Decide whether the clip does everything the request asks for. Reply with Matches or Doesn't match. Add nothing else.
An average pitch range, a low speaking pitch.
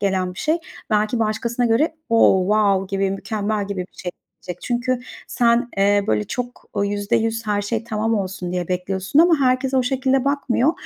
Doesn't match